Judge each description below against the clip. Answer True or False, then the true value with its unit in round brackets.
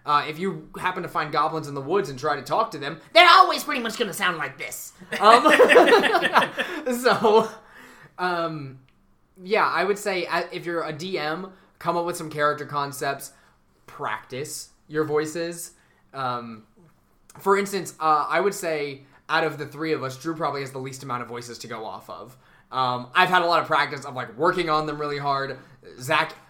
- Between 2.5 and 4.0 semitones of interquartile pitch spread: False (4.5 semitones)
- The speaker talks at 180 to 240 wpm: True (195 wpm)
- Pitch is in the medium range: True (160 Hz)